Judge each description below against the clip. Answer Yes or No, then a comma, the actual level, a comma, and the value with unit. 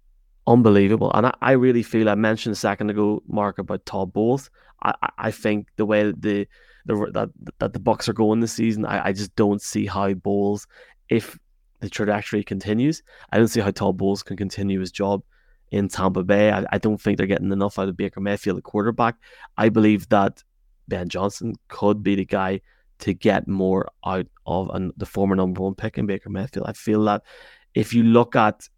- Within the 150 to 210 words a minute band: Yes, fast, 205 wpm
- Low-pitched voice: Yes, low, 105 Hz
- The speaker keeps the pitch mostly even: Yes, narrow, 1.8 semitones